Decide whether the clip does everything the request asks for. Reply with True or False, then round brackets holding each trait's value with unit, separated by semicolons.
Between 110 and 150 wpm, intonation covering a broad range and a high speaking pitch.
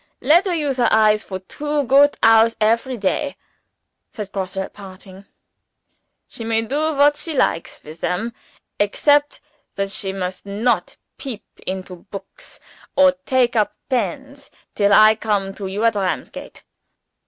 True (145 wpm; 5.9 semitones; 220 Hz)